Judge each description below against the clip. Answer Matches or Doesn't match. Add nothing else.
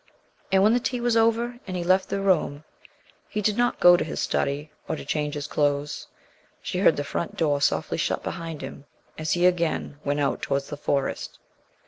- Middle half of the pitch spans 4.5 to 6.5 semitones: Matches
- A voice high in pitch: Doesn't match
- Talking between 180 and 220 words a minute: Matches